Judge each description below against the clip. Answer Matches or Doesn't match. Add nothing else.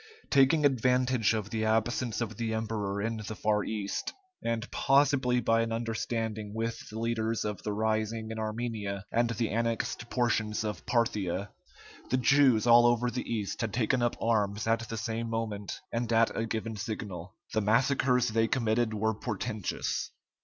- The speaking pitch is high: Doesn't match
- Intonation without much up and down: Matches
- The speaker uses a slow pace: Doesn't match